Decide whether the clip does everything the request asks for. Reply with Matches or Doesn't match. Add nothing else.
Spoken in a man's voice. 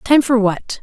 Doesn't match